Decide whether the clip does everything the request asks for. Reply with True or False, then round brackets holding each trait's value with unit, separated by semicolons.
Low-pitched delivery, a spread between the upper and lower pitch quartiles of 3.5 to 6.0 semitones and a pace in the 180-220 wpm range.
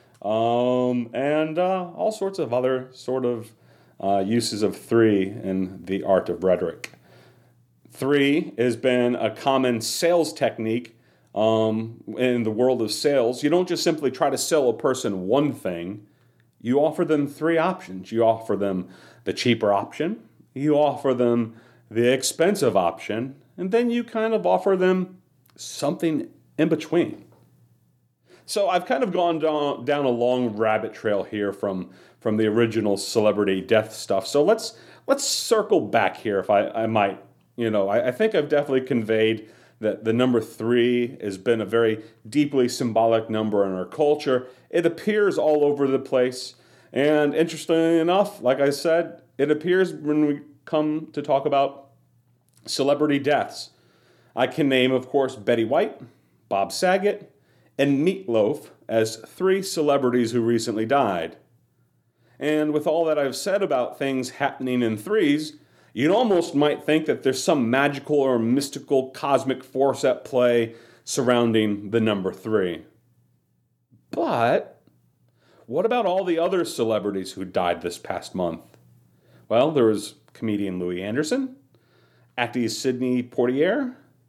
False (125 Hz; 5.2 semitones; 150 wpm)